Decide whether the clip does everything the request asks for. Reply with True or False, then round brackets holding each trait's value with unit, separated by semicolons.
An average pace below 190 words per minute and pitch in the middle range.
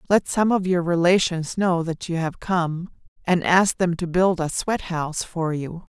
False (200 wpm; 175 Hz)